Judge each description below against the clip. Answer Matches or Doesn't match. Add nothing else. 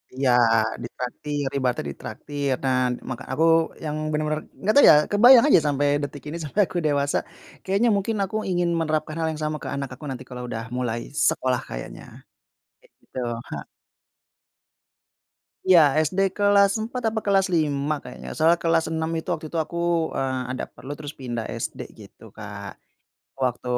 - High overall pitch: Doesn't match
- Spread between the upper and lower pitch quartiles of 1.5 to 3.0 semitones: Doesn't match